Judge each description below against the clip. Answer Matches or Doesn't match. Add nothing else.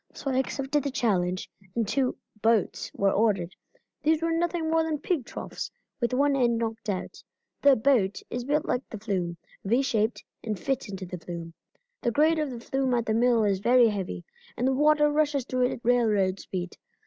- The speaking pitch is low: Doesn't match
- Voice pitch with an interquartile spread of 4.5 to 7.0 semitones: Matches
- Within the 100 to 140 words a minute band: Doesn't match